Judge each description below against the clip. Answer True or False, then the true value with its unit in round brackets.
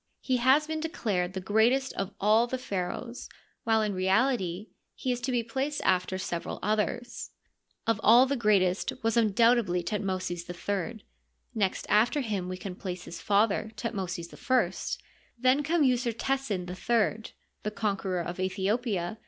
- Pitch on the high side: True (215 Hz)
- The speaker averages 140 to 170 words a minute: True (150 wpm)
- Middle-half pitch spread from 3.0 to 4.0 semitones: False (4.5 semitones)